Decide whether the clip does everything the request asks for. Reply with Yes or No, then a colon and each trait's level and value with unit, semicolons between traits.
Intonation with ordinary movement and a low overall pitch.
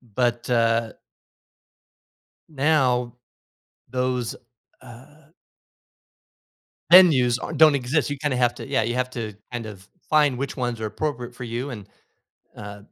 Yes: average, 3.1 semitones; low, 125 Hz